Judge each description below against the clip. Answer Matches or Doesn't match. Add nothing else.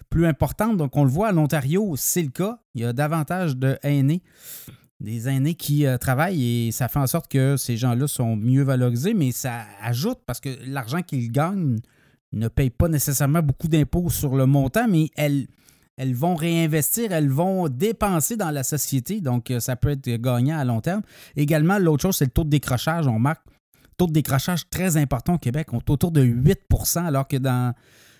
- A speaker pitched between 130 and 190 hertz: Matches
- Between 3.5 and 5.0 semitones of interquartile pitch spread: Matches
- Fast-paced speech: Doesn't match